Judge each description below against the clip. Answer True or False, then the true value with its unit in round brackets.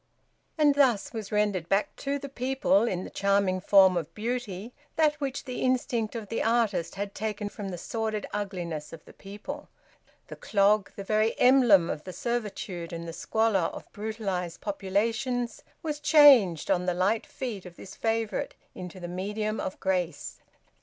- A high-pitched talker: True (210 Hz)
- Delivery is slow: False (165 wpm)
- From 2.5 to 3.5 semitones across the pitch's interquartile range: False (4.1 semitones)